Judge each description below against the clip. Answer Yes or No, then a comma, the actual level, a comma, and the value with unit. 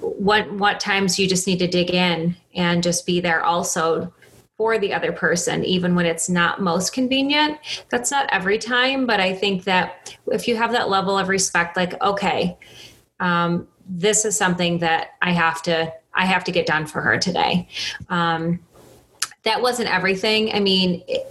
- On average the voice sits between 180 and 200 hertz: Yes, medium, 185 Hz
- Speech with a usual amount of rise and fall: Yes, average, 3.3 semitones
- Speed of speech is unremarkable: Yes, average, 180 wpm